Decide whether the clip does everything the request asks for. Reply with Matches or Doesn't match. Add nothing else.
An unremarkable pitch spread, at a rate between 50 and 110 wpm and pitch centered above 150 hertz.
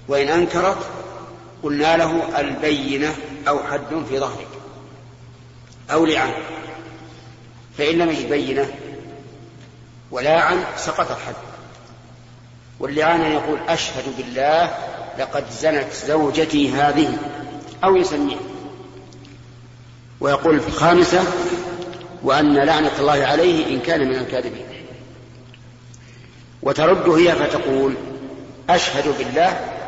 Doesn't match